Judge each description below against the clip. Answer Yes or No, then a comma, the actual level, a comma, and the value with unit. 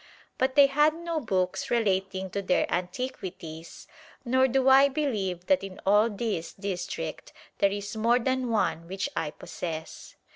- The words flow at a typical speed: Yes, average, 150 wpm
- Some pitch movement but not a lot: No, wide, 5.9 semitones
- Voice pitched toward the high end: Yes, high, 205 Hz